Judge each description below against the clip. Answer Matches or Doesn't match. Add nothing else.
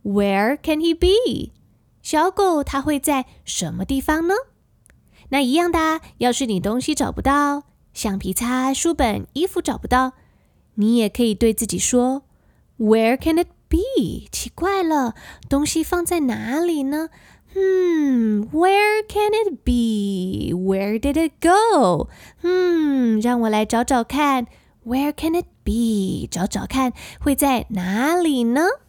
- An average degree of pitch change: Doesn't match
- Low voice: Doesn't match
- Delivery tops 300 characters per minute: Doesn't match